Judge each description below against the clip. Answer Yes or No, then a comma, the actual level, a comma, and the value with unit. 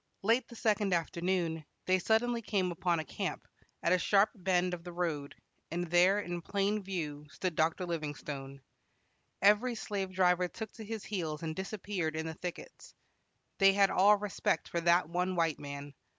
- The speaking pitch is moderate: Yes, medium, 180 Hz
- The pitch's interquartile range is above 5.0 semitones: No, average, 3.5 semitones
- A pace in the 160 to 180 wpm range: Yes, average, 170 wpm